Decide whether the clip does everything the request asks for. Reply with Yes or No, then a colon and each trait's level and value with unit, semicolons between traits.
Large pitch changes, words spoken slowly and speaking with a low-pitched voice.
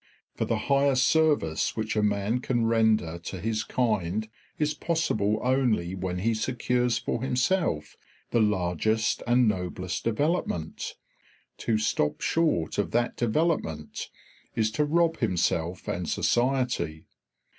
Yes: wide, 5.7 semitones; slow, 125 wpm; low, 110 Hz